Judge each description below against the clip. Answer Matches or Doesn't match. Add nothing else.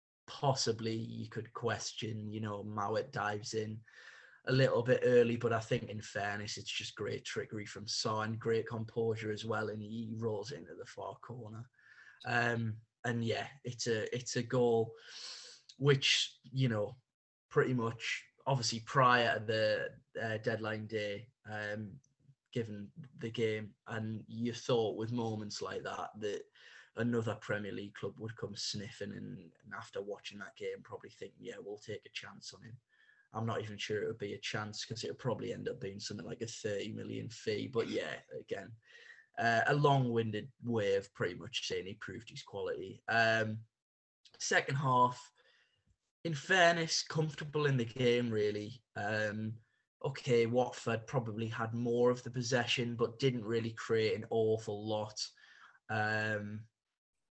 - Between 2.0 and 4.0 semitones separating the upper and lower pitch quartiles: Matches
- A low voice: Matches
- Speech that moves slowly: Doesn't match